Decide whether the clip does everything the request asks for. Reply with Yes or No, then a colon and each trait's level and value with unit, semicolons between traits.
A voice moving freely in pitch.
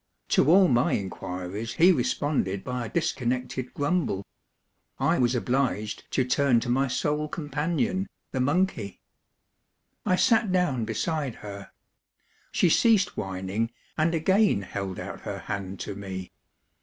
Yes: wide, 8.0 semitones